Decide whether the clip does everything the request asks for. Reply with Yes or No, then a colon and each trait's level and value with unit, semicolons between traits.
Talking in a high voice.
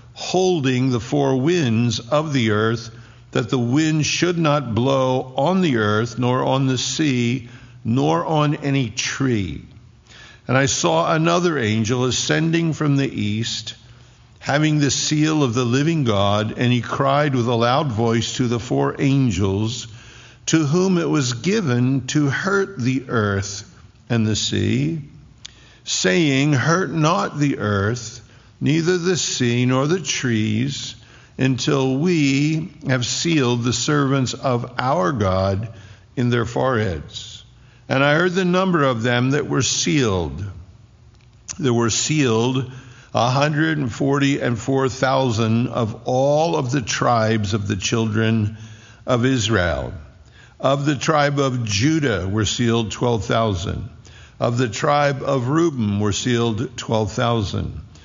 No: low, 125 Hz